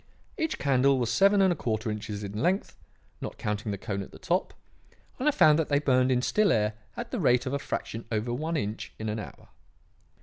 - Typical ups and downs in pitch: No, wide, 6.3 semitones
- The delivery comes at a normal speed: No, fast, 225 wpm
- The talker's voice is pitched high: No, low, 125 Hz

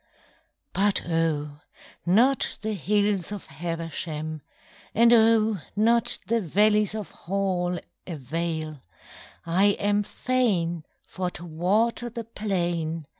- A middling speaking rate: No, slow, 105 wpm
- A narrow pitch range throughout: No, average, 4.4 semitones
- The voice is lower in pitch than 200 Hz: Yes, high, 190 Hz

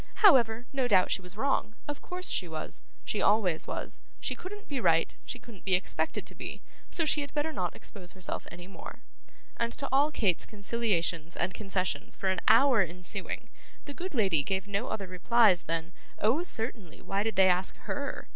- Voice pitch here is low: No, high, 205 Hz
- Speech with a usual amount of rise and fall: No, wide, 6.5 semitones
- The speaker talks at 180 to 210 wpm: Yes, average, 190 wpm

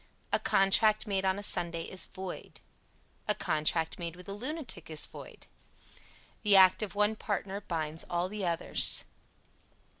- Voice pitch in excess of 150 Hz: Yes, high, 190 Hz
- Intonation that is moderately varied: Yes, average, 3.3 semitones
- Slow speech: No, average, 150 wpm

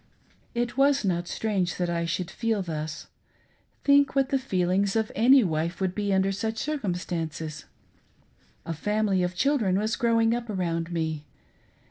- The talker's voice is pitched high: Yes, high, 195 Hz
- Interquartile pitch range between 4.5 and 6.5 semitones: Yes, average, 4.9 semitones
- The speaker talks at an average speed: Yes, average, 150 wpm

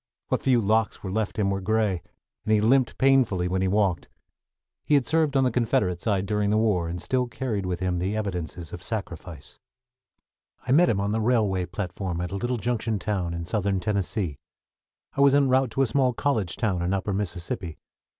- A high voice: No, low, 105 Hz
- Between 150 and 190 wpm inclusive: No, average, 200 wpm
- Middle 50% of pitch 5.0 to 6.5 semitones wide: No, average, 4.5 semitones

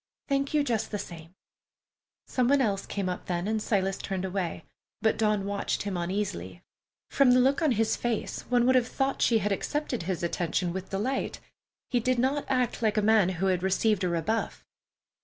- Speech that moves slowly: No, average, 195 wpm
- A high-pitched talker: Yes, high, 210 Hz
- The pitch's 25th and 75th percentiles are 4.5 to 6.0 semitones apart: Yes, average, 4.9 semitones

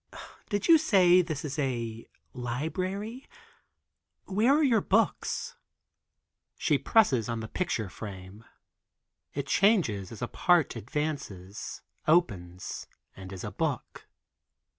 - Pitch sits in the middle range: Yes, medium, 145 Hz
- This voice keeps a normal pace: No, slow, 115 wpm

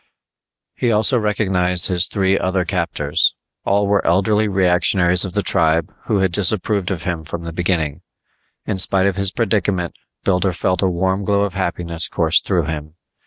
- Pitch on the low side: Yes, very low, 95 Hz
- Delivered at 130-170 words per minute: Yes, average, 165 wpm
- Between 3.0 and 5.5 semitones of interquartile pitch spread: No, narrow, 2.5 semitones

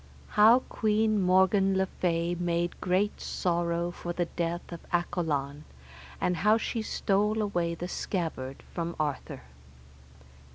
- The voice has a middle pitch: Yes, medium, 175 Hz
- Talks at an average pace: No, slow, 125 wpm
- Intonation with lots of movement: No, average, 2.9 semitones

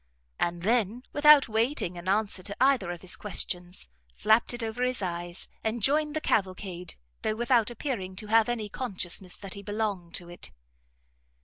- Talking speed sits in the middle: Yes, average, 170 wpm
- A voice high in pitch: Yes, high, 210 Hz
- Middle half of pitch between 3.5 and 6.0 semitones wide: Yes, average, 4.6 semitones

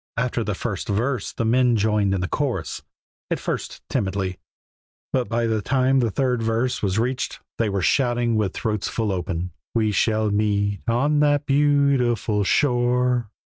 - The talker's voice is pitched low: Yes, low, 115 Hz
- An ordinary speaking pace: Yes, average, 160 wpm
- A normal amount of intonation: Yes, average, 3.5 semitones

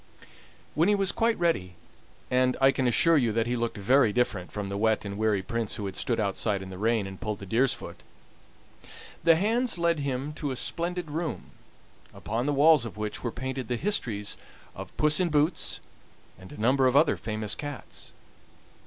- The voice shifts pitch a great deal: Yes, wide, 6.1 semitones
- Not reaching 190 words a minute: No, average, 195 wpm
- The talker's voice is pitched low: Yes, low, 125 Hz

